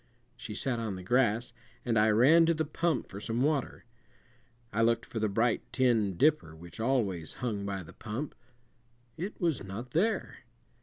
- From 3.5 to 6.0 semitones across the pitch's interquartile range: Yes, average, 5.0 semitones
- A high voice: No, low, 115 Hz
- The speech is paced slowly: No, average, 170 wpm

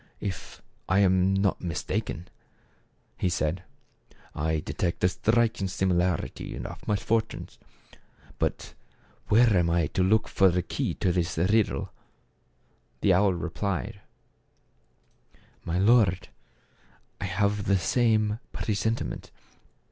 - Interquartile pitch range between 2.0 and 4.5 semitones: Yes, average, 3.1 semitones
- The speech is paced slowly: Yes, slow, 125 wpm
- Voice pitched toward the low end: Yes, very low, 95 Hz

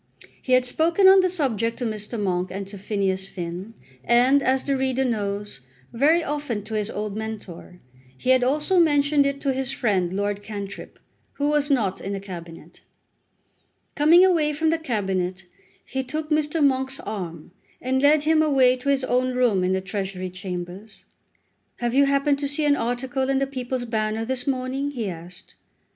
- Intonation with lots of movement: Yes, wide, 5.8 semitones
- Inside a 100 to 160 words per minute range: No, average, 180 wpm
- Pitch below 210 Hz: No, very high, 250 Hz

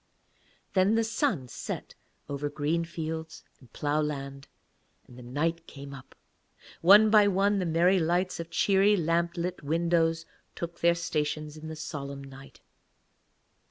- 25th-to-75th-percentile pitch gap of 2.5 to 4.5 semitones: Yes, average, 3.5 semitones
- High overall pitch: No, medium, 165 Hz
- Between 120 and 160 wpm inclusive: Yes, average, 140 wpm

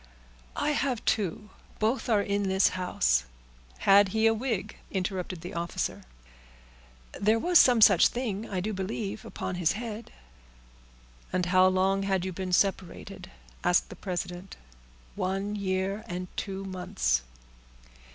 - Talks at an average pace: No, slow, 130 wpm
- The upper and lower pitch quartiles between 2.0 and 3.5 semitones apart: Yes, narrow, 2.6 semitones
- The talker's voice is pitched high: Yes, high, 195 Hz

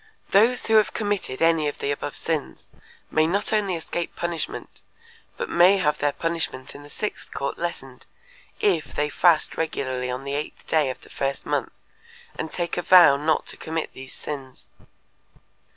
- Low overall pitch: No, medium, 160 Hz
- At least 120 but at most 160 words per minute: No, average, 170 wpm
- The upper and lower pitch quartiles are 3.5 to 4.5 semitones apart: Yes, average, 3.9 semitones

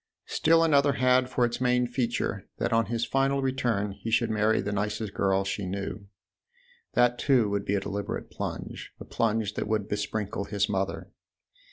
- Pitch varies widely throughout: No, average, 3.5 semitones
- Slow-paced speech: No, average, 175 wpm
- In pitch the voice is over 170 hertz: No, low, 110 Hz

